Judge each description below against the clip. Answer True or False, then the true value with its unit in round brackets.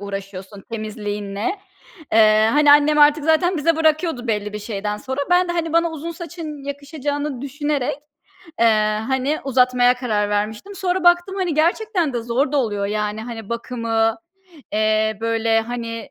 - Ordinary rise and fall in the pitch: False (6.1 semitones)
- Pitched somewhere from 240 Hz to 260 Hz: True (250 Hz)